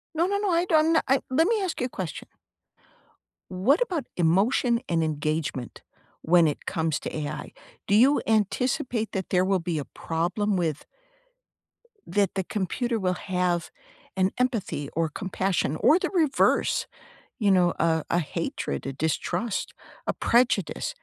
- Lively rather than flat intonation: Yes, wide, 7.4 semitones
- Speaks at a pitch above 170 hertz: Yes, high, 190 Hz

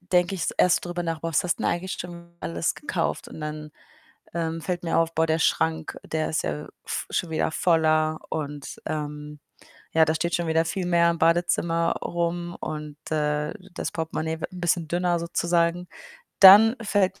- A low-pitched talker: No, medium, 165 Hz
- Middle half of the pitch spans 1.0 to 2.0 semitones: Yes, narrow, 1.7 semitones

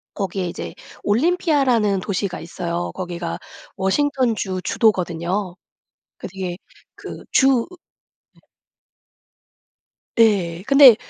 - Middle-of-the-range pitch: No, high, 200 Hz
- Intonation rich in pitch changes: Yes, wide, 6.0 semitones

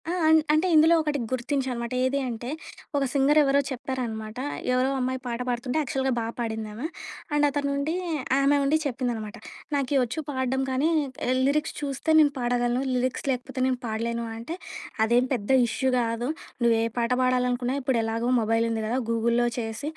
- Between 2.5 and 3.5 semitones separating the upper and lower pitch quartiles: Yes, average, 2.9 semitones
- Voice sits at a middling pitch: No, very high, 250 Hz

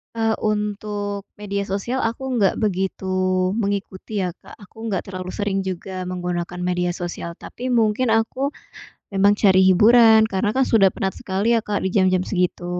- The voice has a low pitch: No, high, 195 Hz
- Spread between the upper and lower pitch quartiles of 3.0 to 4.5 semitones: No, narrow, 2.4 semitones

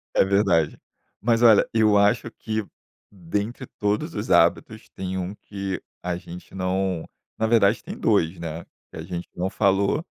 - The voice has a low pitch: Yes, low, 100 Hz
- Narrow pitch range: No, average, 3.2 semitones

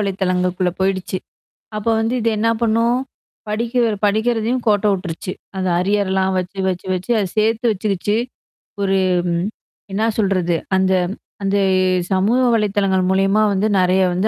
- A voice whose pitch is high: Yes, high, 195 Hz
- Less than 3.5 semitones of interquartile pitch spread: Yes, narrow, 2.5 semitones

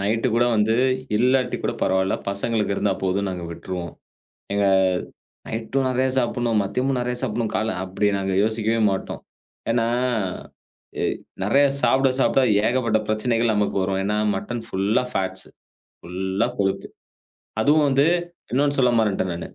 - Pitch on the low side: Yes, low, 110 Hz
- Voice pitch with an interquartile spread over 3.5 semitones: Yes, average, 4.0 semitones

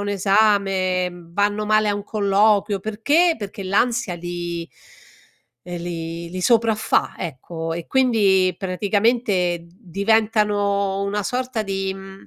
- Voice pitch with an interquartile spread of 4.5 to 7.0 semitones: No, average, 2.8 semitones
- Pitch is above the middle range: Yes, high, 200 Hz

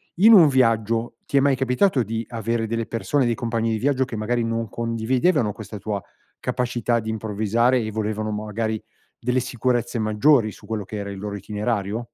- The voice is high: No, low, 115 Hz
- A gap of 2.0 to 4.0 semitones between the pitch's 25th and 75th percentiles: Yes, narrow, 2.5 semitones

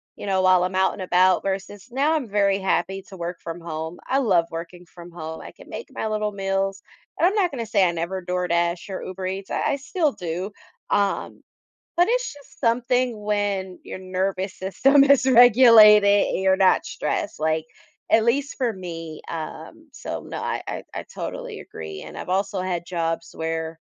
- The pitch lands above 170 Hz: Yes, high, 190 Hz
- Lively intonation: No, average, 4.1 semitones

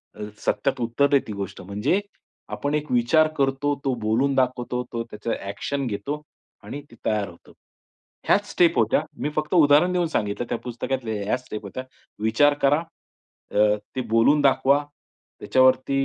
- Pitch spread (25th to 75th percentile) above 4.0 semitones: Yes, average, 4.4 semitones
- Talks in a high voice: No, low, 130 Hz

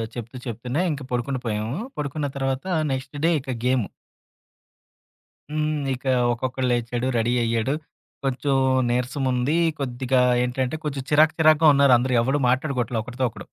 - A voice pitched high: No, low, 130 Hz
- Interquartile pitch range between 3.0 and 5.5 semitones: No, narrow, 2.5 semitones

